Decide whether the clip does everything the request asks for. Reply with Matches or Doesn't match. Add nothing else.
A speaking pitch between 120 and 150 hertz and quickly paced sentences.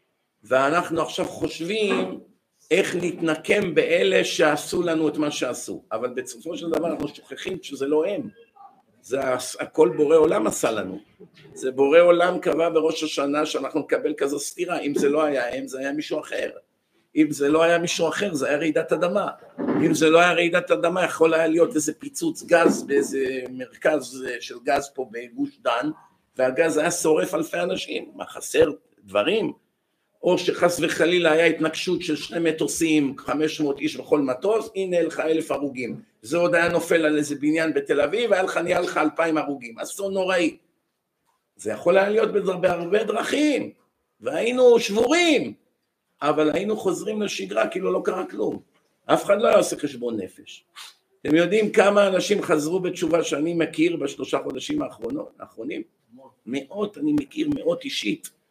Doesn't match